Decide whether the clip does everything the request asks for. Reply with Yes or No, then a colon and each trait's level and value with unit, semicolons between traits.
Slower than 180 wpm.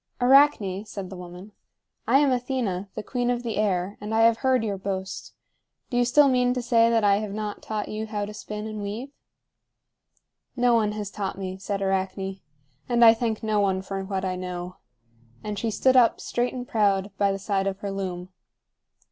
No: average, 200 wpm